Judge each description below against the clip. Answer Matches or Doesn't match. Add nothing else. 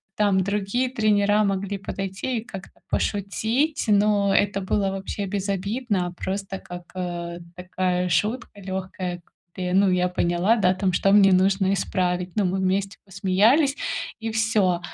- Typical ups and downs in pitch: Doesn't match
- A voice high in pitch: Matches